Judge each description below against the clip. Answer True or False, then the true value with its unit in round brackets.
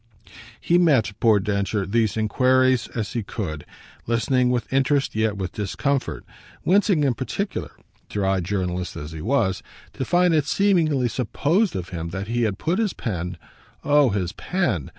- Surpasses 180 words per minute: False (155 wpm)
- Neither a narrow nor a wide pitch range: False (6.5 semitones)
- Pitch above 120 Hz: False (115 Hz)